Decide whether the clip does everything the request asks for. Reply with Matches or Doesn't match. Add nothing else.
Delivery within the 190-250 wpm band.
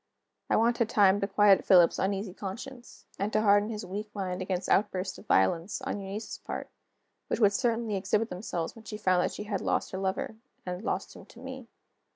Matches